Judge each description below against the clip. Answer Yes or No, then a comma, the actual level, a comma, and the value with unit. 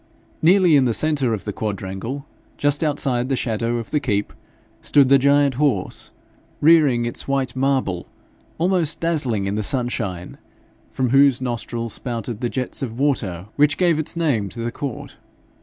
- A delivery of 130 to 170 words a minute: Yes, average, 160 wpm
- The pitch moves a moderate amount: Yes, average, 3.9 semitones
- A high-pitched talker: No, low, 130 Hz